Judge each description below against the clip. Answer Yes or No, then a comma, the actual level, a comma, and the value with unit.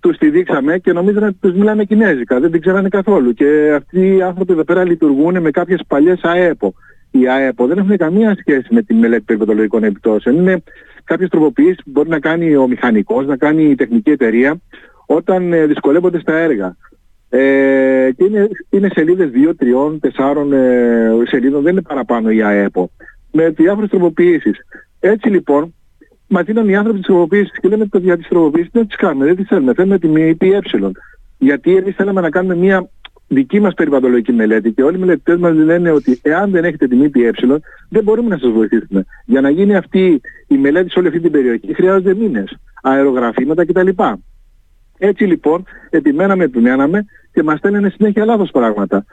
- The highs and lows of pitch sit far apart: Yes, wide, 6.9 semitones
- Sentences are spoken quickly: Yes, fast, 175 wpm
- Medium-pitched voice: Yes, medium, 170 Hz